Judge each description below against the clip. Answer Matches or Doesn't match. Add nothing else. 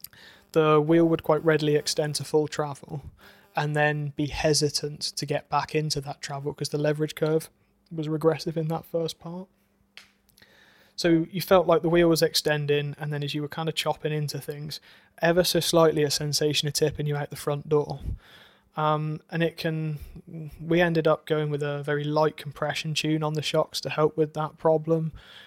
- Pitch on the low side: Doesn't match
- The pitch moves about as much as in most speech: Doesn't match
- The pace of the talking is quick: Doesn't match